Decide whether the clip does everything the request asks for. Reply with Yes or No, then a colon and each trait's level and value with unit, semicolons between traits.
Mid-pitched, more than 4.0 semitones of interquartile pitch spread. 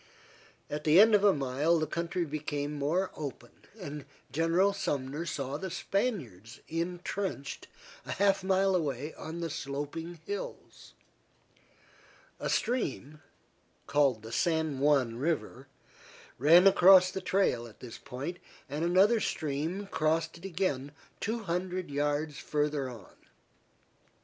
Yes: medium, 160 Hz; average, 4.6 semitones